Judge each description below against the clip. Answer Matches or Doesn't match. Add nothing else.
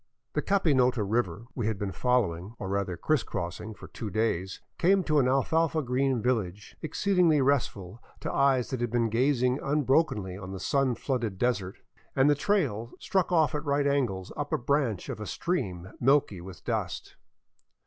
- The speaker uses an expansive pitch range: Matches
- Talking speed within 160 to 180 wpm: Matches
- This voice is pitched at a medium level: Doesn't match